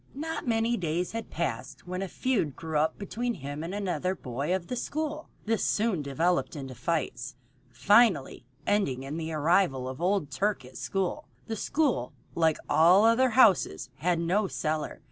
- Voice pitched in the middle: Yes, medium, 180 Hz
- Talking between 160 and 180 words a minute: Yes, average, 170 wpm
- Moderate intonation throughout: No, wide, 6.5 semitones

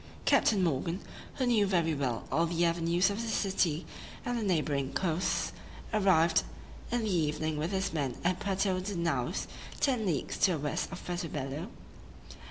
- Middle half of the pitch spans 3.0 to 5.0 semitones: Yes, average, 3.7 semitones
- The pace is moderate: Yes, average, 170 wpm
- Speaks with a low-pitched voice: No, medium, 175 Hz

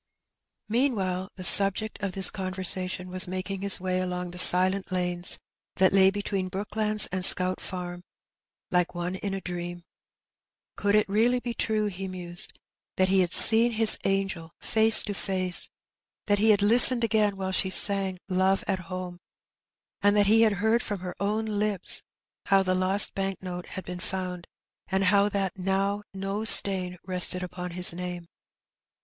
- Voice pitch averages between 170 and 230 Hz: Yes, high, 190 Hz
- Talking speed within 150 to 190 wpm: Yes, average, 165 wpm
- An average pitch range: No, narrow, 2.0 semitones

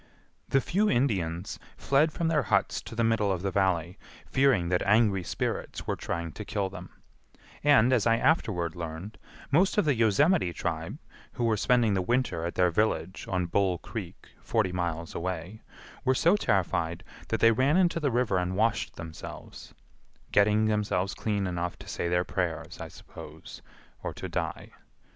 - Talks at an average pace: Yes, average, 165 wpm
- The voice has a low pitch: Yes, low, 100 Hz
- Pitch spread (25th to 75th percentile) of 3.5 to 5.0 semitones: No, wide, 5.4 semitones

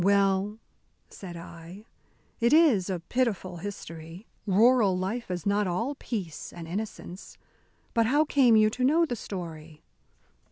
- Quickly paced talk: No, slow, 135 wpm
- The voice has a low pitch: No, high, 200 Hz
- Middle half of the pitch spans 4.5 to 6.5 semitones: Yes, average, 4.9 semitones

